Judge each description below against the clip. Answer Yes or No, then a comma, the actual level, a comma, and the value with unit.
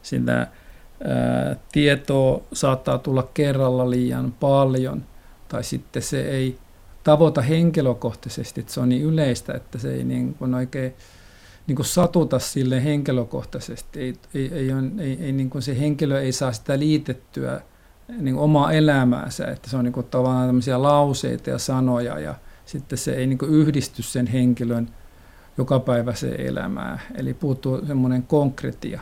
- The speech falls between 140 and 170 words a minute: Yes, average, 145 wpm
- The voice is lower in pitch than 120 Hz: No, low, 130 Hz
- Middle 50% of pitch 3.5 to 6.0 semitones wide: No, narrow, 2.5 semitones